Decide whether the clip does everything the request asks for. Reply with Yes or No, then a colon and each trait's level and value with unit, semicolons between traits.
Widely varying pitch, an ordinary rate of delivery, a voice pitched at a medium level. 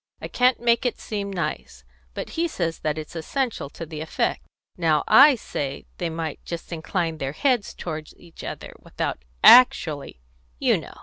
Yes: wide, 7.1 semitones; average, 175 wpm; medium, 165 Hz